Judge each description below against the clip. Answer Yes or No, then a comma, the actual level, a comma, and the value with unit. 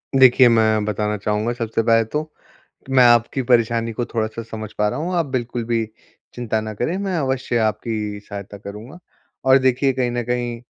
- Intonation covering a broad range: No, average, 2.8 semitones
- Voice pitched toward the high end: No, low, 115 Hz